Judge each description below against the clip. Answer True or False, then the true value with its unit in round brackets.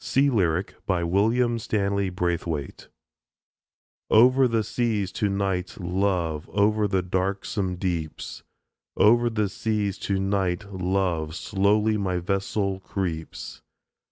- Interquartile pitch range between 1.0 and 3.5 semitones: True (2.8 semitones)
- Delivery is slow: True (105 wpm)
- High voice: False (100 Hz)